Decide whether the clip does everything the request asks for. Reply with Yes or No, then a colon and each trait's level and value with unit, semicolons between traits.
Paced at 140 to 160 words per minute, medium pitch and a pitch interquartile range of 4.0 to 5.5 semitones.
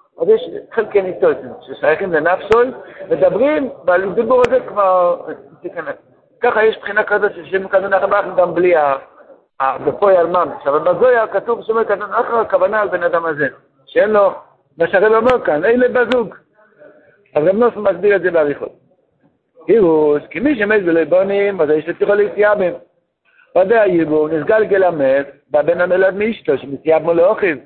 No: fast, 150 wpm; high, 200 Hz; average, 4.8 semitones